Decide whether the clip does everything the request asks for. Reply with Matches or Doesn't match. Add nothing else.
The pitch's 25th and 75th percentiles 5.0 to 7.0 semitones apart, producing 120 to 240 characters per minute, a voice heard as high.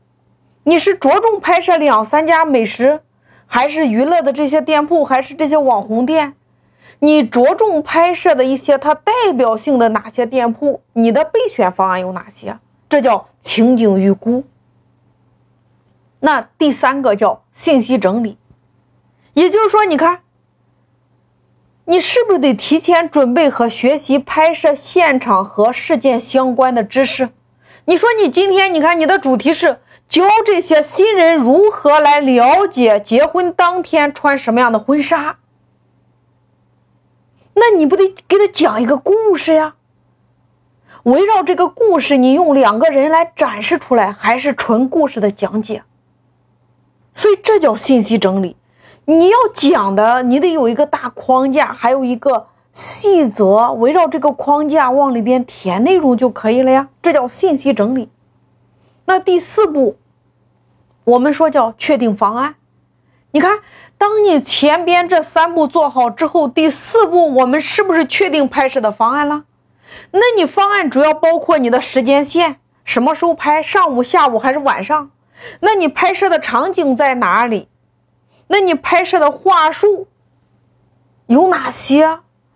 Matches